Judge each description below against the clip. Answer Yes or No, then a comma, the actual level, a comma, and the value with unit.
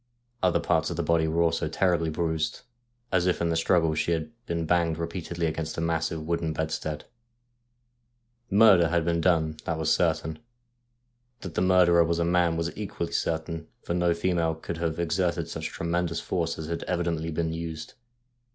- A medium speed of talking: Yes, average, 180 wpm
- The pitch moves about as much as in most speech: No, narrow, 1.2 semitones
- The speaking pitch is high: No, very low, 85 Hz